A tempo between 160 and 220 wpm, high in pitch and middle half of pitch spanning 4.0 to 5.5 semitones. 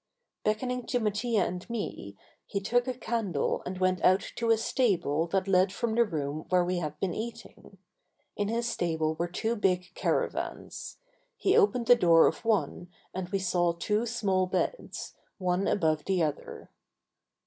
Yes: average, 165 wpm; high, 195 Hz; average, 4.7 semitones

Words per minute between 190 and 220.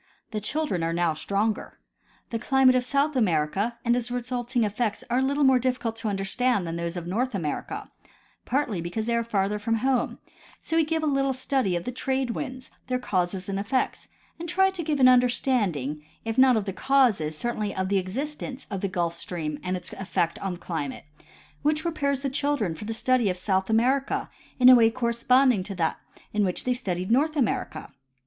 Yes: average, 195 wpm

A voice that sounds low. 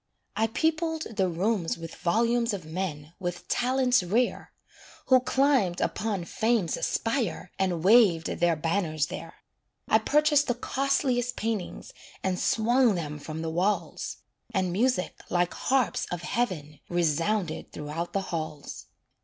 No: high, 195 Hz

